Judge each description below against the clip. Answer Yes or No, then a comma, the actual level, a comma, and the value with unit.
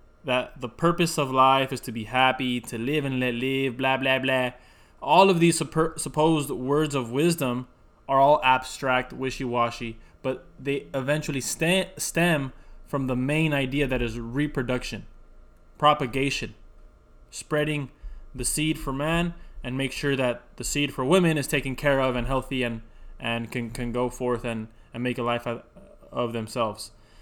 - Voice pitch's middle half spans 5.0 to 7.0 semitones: No, average, 3.3 semitones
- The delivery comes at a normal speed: Yes, average, 170 wpm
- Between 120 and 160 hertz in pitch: Yes, low, 130 Hz